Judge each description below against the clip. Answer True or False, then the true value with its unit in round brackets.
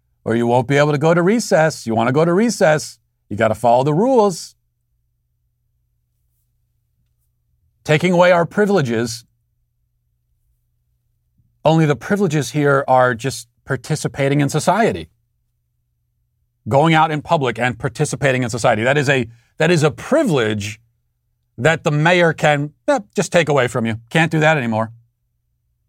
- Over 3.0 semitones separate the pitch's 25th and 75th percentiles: True (5.2 semitones)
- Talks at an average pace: True (145 wpm)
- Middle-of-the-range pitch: False (125 Hz)